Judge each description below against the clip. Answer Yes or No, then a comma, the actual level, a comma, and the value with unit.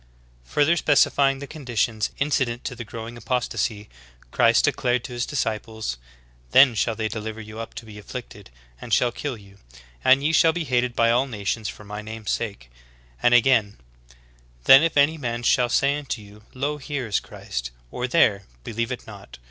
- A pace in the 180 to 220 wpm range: Yes, average, 185 wpm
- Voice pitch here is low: Yes, low, 120 Hz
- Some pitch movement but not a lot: Yes, average, 3.9 semitones